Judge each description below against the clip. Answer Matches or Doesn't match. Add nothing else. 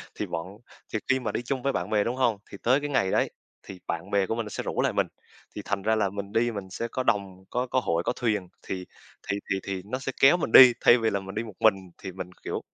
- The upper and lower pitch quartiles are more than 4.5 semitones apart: Doesn't match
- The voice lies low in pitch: Matches